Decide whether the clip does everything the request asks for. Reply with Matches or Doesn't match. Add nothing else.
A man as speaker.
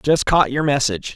Matches